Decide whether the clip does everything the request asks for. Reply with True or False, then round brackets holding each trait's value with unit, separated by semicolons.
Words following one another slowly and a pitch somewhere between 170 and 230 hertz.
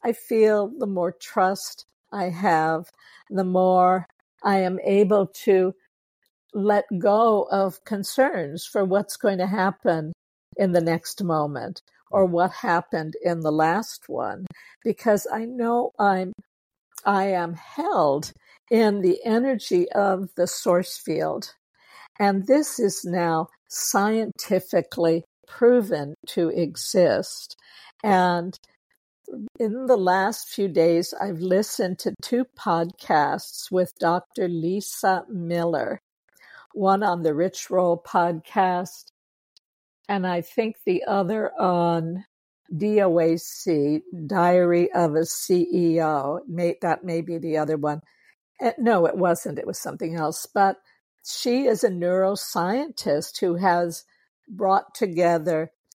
True (115 wpm; 185 Hz)